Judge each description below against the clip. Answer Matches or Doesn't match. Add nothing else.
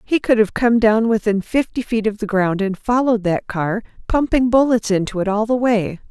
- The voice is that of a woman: Matches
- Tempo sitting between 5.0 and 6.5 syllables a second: Matches